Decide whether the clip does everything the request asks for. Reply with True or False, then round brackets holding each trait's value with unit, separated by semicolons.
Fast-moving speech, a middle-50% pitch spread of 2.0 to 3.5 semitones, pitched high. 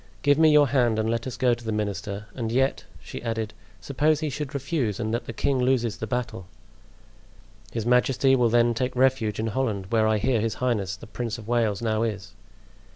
False (210 wpm; 3.1 semitones; 120 Hz)